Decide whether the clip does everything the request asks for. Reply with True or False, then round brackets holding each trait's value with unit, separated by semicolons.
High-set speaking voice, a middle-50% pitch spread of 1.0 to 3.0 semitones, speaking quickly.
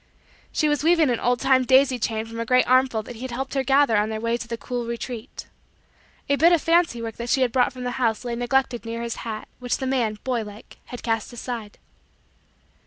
True (245 Hz; 2.4 semitones; 235 wpm)